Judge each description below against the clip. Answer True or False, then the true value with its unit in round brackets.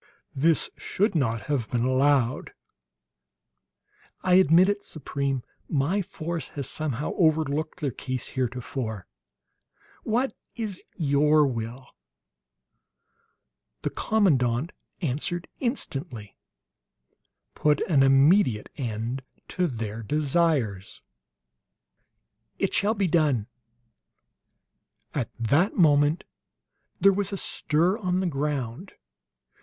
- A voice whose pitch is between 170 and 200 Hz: False (145 Hz)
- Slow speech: True (95 wpm)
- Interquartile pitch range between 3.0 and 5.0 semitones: False (5.5 semitones)